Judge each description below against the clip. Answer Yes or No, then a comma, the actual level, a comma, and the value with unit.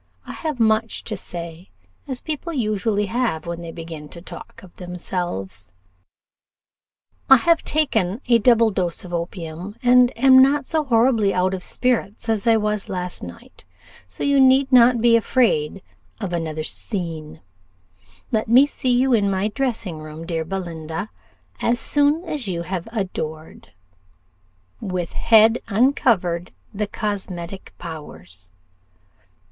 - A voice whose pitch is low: No, high, 205 Hz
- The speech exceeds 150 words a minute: No, average, 140 wpm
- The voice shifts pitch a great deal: Yes, wide, 6.0 semitones